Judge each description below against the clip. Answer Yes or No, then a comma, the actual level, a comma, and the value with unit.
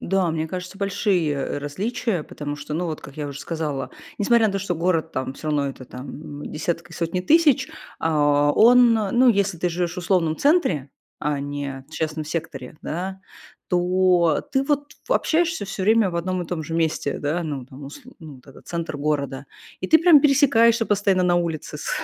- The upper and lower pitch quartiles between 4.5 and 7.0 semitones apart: Yes, average, 5.1 semitones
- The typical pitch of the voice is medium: Yes, medium, 170 Hz